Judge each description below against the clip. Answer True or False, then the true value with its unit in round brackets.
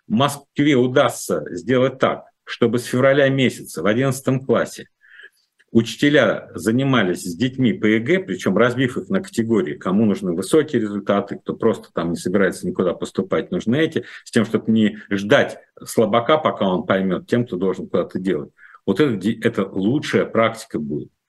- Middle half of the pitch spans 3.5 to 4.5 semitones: True (3.8 semitones)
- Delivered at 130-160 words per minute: True (155 wpm)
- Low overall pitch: True (120 Hz)